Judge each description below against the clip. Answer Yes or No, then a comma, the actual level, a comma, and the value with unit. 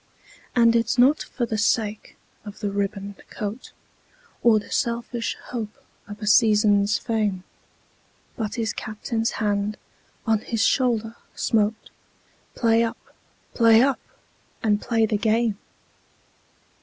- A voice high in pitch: Yes, high, 220 Hz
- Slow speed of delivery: Yes, slow, 120 wpm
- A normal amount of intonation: No, narrow, 1.9 semitones